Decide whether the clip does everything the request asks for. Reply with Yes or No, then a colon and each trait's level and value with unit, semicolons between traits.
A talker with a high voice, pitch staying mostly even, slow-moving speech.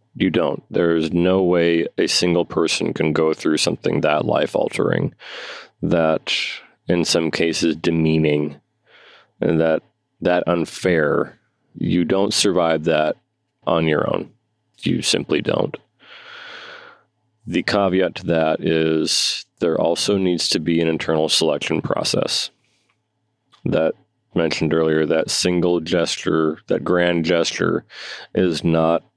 No: very low, 85 Hz; narrow, 2.0 semitones; slow, 120 wpm